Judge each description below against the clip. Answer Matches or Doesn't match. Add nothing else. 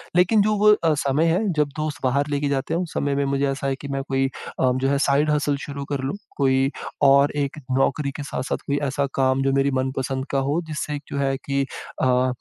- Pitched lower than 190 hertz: Matches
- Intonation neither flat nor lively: Doesn't match